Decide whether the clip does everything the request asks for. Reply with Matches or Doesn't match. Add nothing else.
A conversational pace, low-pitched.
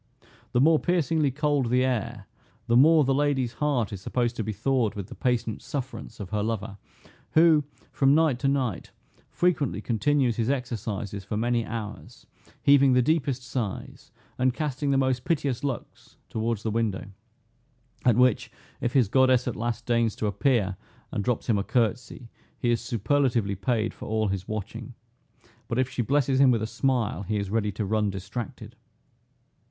Matches